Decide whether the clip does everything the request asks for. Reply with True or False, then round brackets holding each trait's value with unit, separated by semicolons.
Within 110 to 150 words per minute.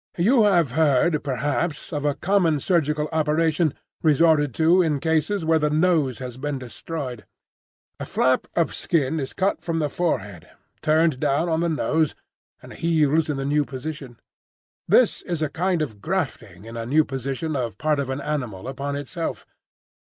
False (165 wpm)